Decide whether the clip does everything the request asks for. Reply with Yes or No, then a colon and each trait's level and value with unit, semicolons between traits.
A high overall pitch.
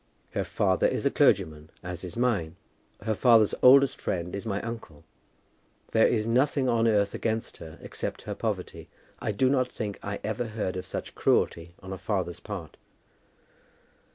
No: low, 105 Hz